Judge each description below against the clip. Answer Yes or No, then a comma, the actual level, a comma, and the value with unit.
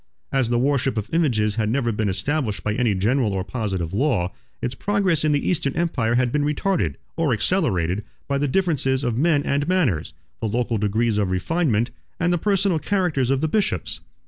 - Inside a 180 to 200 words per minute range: Yes, average, 190 wpm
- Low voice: Yes, low, 130 Hz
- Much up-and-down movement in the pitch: Yes, wide, 6.5 semitones